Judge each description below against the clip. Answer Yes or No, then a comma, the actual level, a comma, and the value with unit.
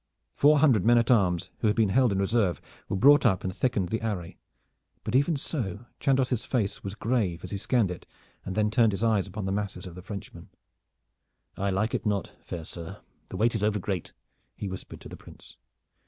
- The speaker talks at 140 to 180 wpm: No, fast, 205 wpm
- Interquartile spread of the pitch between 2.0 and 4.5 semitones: Yes, average, 3.8 semitones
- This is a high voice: No, low, 105 Hz